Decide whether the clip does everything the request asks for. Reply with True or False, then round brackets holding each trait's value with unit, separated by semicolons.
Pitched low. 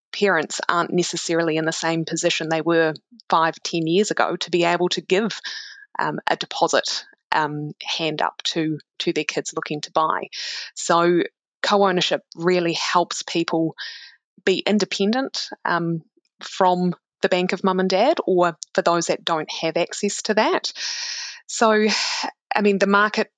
False (175 Hz)